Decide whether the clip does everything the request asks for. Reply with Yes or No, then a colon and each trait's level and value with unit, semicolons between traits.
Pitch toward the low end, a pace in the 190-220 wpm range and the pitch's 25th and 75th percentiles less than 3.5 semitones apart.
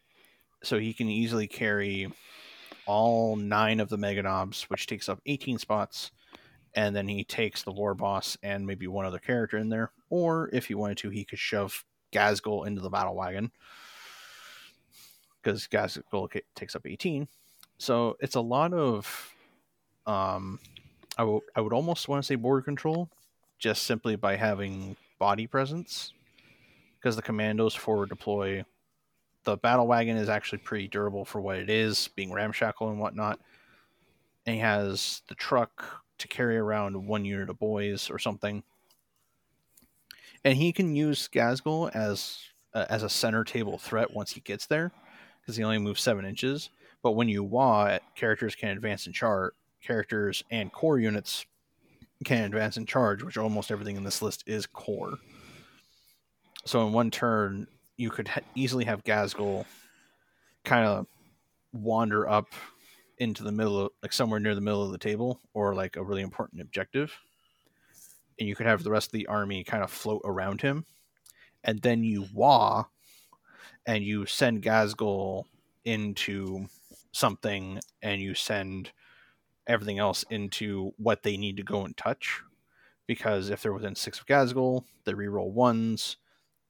No: low, 105 Hz; average, 160 wpm; narrow, 2.6 semitones